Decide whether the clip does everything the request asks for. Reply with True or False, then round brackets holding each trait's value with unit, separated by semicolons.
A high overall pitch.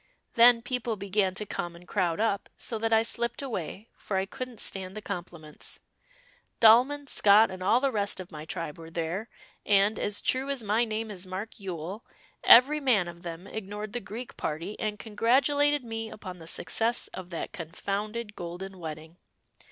True (205 Hz)